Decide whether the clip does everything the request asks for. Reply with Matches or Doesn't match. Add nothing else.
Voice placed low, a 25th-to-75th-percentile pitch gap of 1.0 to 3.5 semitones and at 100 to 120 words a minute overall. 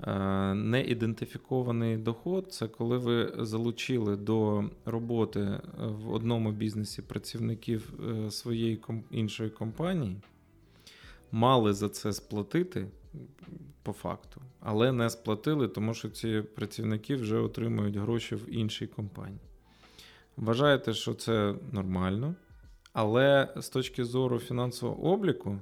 Matches